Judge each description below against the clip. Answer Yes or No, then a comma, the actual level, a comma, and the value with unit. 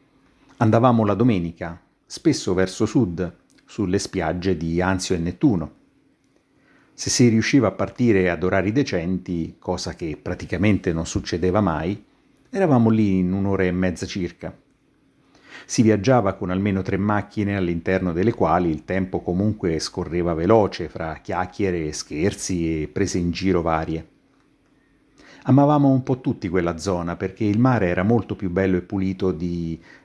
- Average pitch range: Yes, average, 3.1 semitones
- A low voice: Yes, very low, 95 Hz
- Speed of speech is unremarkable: Yes, average, 145 wpm